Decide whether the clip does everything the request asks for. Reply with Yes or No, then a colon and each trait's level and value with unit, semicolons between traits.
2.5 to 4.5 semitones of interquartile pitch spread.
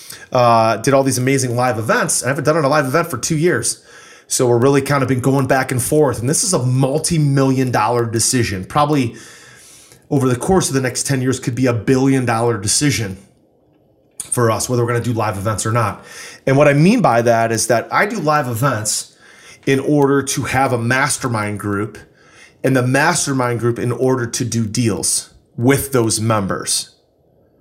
Yes: average, 2.9 semitones